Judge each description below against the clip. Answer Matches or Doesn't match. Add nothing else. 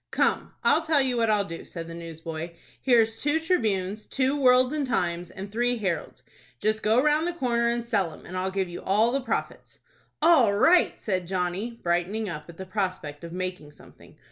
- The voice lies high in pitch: Matches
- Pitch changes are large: Matches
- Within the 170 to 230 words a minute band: Matches